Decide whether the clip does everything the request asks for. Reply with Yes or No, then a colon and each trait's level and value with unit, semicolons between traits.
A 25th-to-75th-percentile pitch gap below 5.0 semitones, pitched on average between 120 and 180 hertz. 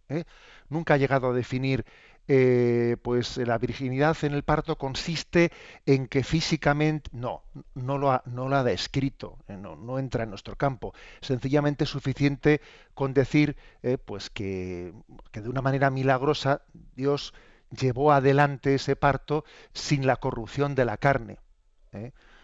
Yes: narrow, 2.6 semitones; low, 135 Hz